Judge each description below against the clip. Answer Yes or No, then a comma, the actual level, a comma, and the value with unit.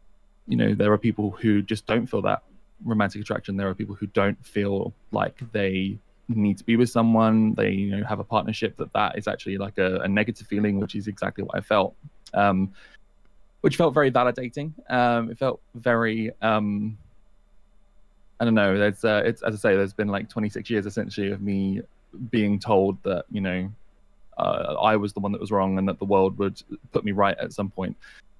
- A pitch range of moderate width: No, narrow, 1.9 semitones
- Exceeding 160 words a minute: Yes, fast, 205 wpm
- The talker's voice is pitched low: Yes, low, 105 Hz